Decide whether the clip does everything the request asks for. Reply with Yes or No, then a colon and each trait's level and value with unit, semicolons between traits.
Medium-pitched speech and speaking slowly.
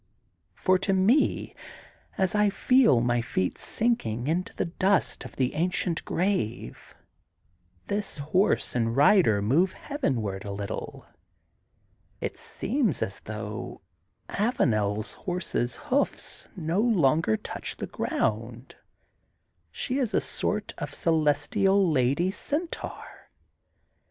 Yes: medium, 165 Hz; slow, 110 wpm